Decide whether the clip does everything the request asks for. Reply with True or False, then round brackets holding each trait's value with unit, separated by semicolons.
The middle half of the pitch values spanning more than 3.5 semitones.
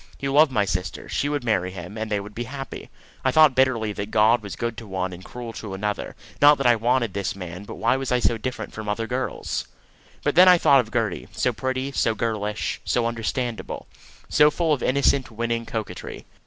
True (3.9 semitones)